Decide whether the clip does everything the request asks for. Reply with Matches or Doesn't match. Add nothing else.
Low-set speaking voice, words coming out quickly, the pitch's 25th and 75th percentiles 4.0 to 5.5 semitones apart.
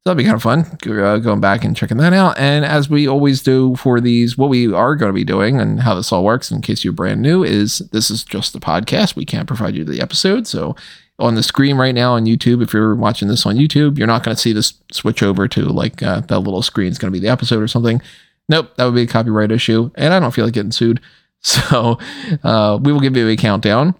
Matches